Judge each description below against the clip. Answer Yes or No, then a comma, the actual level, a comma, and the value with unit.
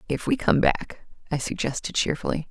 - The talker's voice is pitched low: No, medium, 160 Hz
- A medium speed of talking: Yes, average, 165 wpm